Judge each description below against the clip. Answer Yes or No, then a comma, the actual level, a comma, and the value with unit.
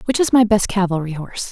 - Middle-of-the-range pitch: No, high, 200 Hz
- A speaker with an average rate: No, fast, 240 wpm